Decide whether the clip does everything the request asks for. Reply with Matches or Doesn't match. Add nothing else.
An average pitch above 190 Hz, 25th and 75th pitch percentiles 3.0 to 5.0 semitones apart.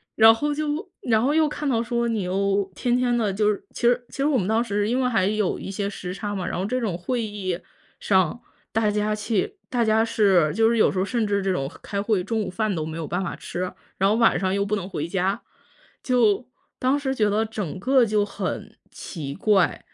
Matches